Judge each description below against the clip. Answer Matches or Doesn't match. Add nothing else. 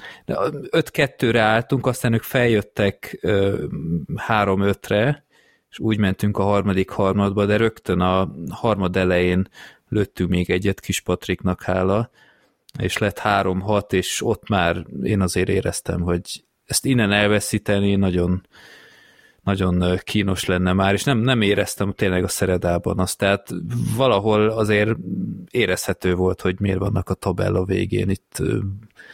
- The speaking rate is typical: Matches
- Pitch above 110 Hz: Doesn't match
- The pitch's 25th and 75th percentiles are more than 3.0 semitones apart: Doesn't match